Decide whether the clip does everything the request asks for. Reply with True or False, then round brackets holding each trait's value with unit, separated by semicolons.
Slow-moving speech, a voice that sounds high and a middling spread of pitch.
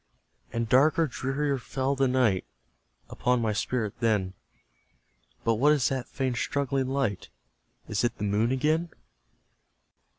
False (130 wpm; 130 Hz; 3.3 semitones)